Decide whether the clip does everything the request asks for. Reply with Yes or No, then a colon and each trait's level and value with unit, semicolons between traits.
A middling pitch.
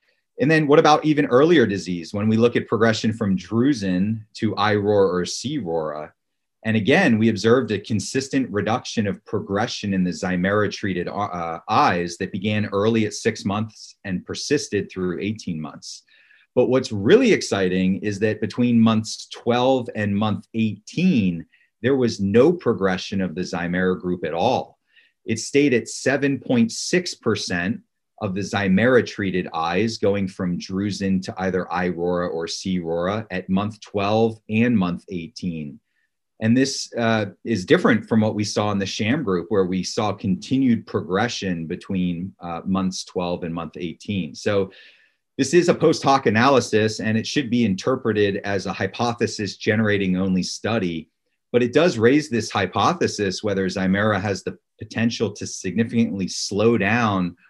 No: low, 105 Hz